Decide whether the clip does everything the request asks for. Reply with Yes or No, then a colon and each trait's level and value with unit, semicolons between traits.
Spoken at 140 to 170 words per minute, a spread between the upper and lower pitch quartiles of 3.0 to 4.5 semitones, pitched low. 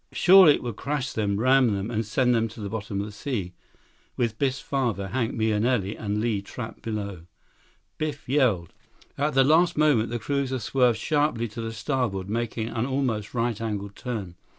No: average, 180 wpm; average, 4.0 semitones; low, 115 Hz